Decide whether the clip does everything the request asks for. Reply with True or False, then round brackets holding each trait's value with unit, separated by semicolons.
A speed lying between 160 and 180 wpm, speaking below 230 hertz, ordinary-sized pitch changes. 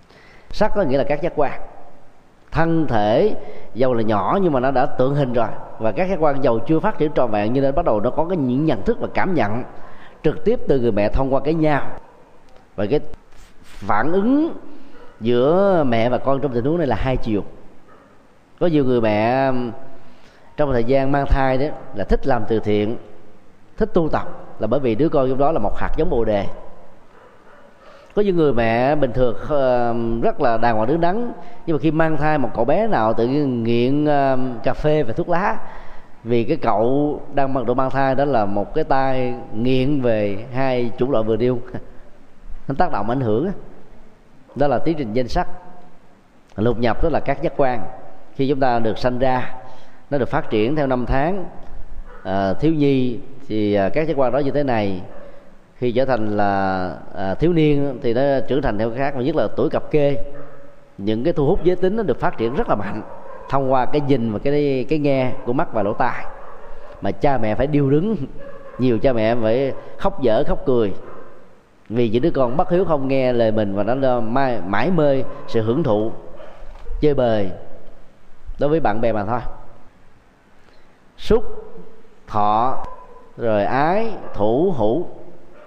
False (195 wpm; 135 Hz; 4.6 semitones)